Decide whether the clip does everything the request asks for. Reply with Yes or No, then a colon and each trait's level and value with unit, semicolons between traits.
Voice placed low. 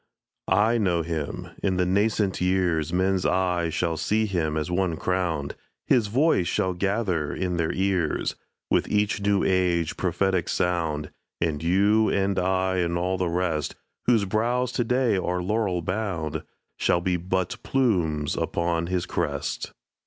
Yes: very low, 90 Hz